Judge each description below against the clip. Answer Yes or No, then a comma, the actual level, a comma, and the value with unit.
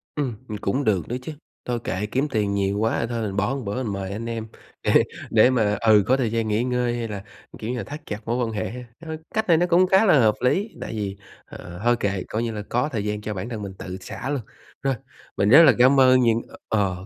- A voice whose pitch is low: Yes, low, 115 Hz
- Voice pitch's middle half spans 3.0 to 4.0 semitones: Yes, average, 3.7 semitones